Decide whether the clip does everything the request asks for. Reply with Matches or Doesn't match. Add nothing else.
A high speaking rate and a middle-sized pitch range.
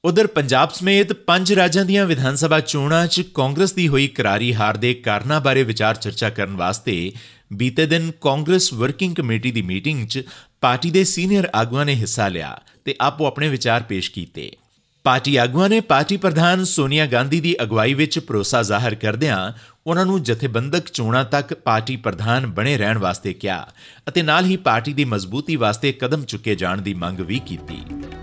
Doesn't match